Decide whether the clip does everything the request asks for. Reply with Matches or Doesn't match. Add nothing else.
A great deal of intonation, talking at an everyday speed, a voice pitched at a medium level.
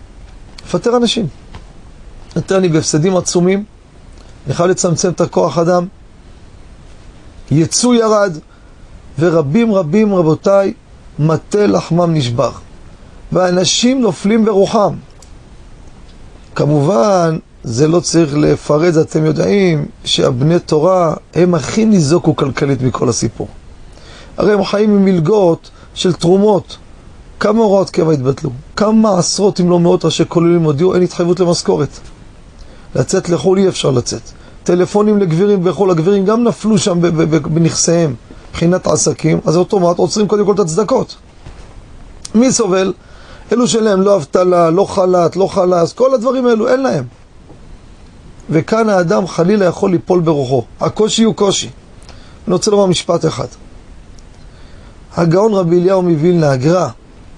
Doesn't match